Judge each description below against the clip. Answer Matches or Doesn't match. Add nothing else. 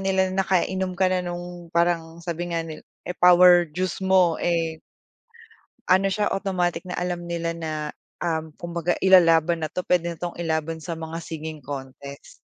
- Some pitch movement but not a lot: Doesn't match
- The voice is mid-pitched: Matches